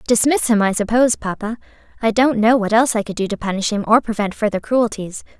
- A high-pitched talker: Yes, high, 220 Hz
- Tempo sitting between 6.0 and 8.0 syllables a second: Yes, 6.2 syllables/s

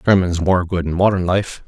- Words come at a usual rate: No, fast, 215 wpm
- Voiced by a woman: No, male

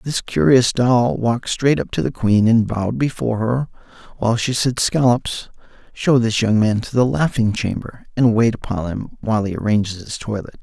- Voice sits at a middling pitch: No, low, 115 Hz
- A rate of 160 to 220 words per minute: Yes, average, 190 wpm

